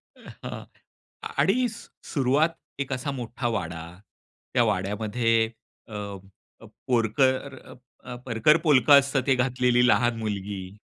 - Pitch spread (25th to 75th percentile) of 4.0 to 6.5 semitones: No, average, 3.3 semitones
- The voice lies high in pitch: No, low, 125 Hz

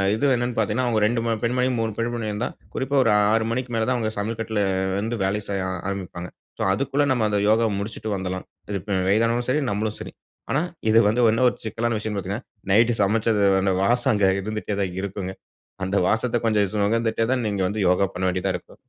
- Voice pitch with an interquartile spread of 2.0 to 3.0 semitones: Yes, average, 2.7 semitones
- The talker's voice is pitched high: No, low, 110 Hz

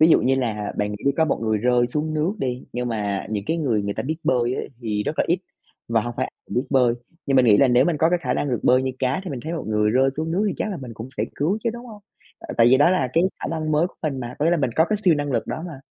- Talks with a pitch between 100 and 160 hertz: Yes, low, 135 Hz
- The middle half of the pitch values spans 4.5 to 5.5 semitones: Yes, average, 5.0 semitones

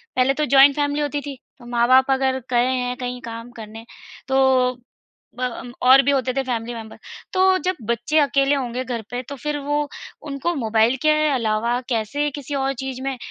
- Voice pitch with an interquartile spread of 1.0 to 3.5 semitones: Yes, narrow, 2.5 semitones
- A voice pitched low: No, very high, 260 Hz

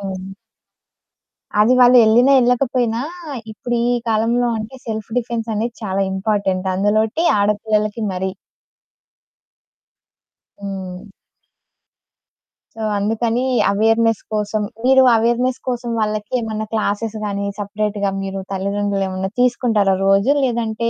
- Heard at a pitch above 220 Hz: No, high, 215 Hz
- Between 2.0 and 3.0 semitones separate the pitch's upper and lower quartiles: Yes, average, 2.7 semitones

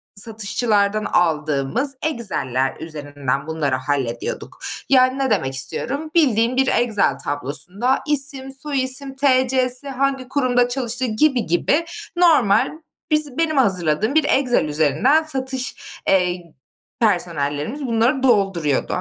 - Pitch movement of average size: No, wide, 8.9 semitones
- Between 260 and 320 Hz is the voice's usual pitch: No, high, 235 Hz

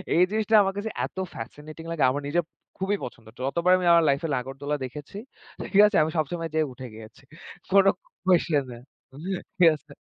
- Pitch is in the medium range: Yes, medium, 155 Hz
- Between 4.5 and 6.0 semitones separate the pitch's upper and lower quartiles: Yes, average, 5.1 semitones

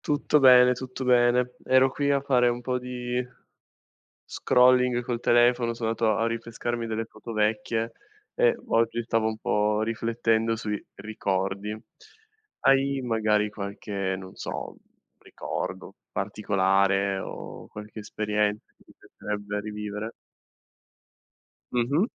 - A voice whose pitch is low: Yes, low, 115 Hz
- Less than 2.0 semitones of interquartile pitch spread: No, average, 2.9 semitones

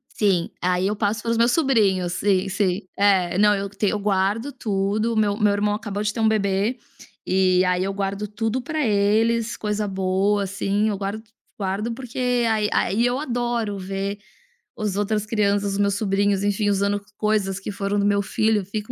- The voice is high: Yes, high, 205 Hz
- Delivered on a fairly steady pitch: Yes, narrow, 1.8 semitones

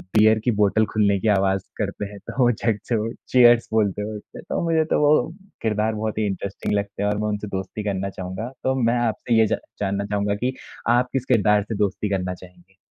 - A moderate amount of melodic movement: No, narrow, 2.3 semitones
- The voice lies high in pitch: No, low, 105 Hz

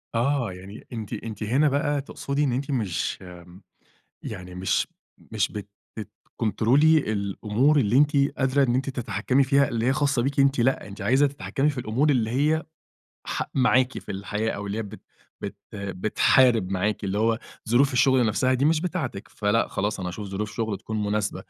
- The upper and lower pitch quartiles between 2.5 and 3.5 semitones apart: No, average, 4.8 semitones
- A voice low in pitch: Yes, low, 115 Hz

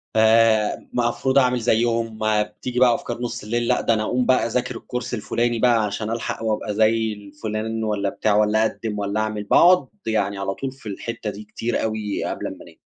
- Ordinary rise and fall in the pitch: No, narrow, 2.0 semitones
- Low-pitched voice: Yes, low, 110 Hz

